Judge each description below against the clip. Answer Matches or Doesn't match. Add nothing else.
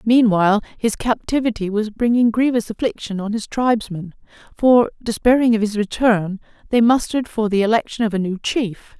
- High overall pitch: Matches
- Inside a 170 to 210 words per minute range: Doesn't match